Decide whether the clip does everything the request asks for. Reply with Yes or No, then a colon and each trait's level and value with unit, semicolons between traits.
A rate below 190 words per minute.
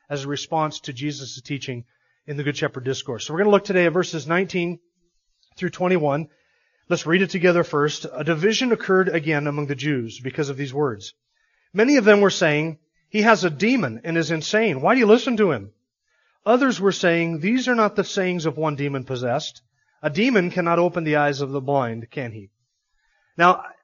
No: average, 200 wpm